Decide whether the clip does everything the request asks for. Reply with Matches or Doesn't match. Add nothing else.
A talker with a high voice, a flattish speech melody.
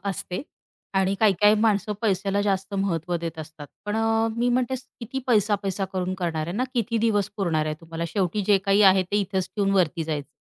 Doesn't match